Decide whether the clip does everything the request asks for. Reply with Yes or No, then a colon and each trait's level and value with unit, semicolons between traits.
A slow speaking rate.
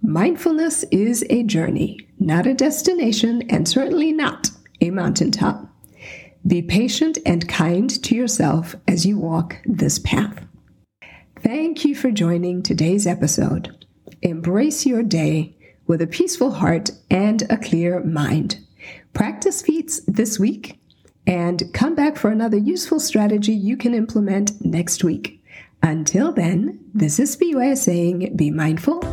Yes: slow, 130 wpm